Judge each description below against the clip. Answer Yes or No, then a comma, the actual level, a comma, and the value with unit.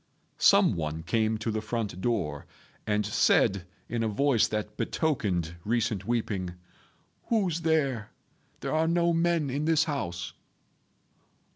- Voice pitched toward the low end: Yes, low, 115 Hz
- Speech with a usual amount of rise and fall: No, wide, 7.8 semitones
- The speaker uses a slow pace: Yes, slow, 130 wpm